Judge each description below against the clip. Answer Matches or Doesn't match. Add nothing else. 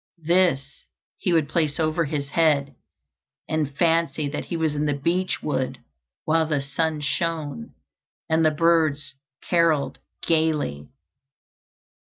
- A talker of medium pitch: Matches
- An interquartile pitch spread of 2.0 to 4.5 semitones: Matches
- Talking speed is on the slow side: Matches